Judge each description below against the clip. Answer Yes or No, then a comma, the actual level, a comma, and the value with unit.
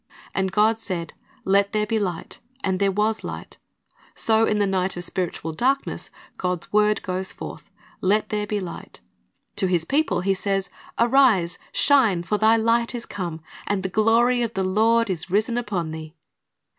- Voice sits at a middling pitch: No, high, 205 Hz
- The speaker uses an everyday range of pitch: Yes, average, 3.3 semitones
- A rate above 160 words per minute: Yes, average, 175 wpm